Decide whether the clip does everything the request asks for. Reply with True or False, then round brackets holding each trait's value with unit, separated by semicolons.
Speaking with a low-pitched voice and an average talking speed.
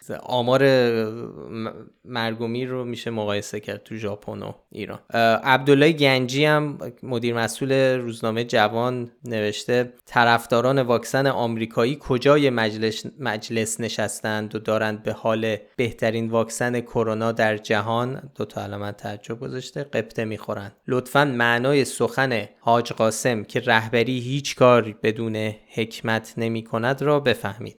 True (115 Hz; 120 wpm)